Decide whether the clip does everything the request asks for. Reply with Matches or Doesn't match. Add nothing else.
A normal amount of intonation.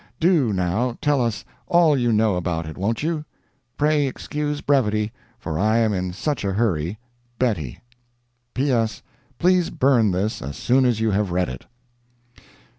Doesn't match